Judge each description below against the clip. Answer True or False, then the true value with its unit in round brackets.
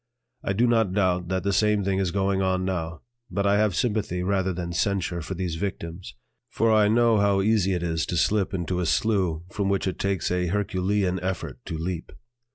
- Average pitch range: False (2.3 semitones)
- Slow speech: False (205 wpm)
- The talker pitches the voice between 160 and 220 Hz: False (95 Hz)